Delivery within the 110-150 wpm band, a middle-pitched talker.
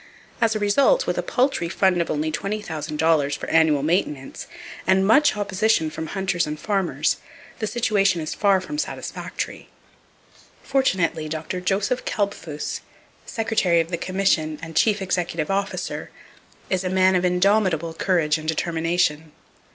Yes: average, 140 wpm; medium, 180 Hz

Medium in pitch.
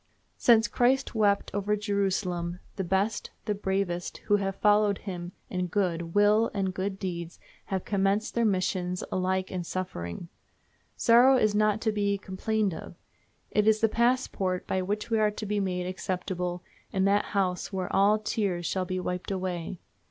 No: high, 195 Hz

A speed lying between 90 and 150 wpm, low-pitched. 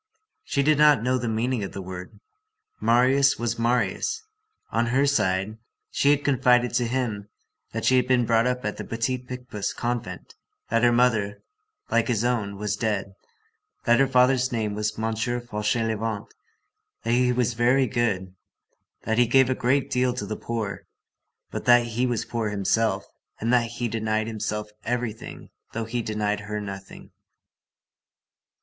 No: average, 160 wpm; low, 115 Hz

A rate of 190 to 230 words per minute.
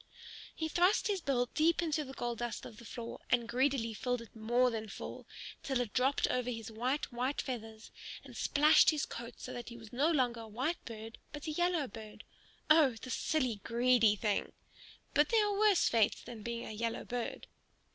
Yes: average, 195 wpm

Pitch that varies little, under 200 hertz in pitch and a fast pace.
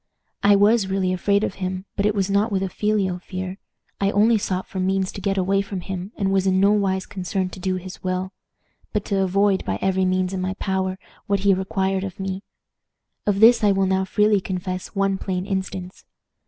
Yes: narrow, 1.2 semitones; high, 190 Hz; fast, 210 wpm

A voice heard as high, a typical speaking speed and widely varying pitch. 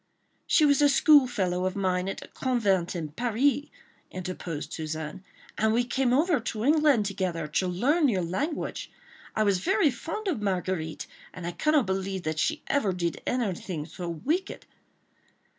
Yes: high, 200 Hz; average, 160 wpm; wide, 7.5 semitones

